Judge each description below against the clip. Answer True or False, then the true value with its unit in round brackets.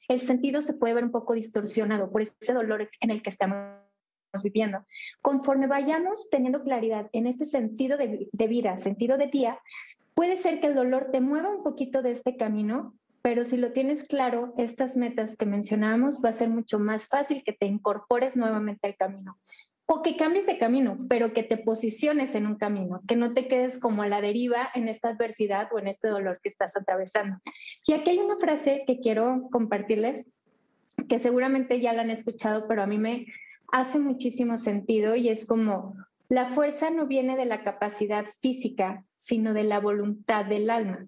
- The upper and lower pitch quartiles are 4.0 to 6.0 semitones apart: False (3.6 semitones)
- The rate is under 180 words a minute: False (190 wpm)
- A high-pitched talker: True (235 Hz)